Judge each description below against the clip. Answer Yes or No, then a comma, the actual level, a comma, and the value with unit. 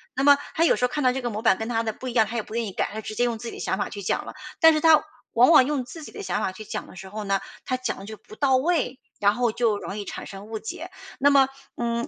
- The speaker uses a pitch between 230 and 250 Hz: Yes, high, 235 Hz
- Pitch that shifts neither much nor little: Yes, average, 3.7 semitones